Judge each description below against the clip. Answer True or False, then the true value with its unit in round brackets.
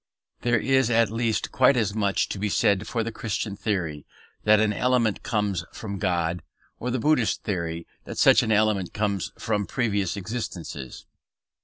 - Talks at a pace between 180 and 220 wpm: False (165 wpm)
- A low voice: True (105 Hz)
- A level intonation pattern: False (3.0 semitones)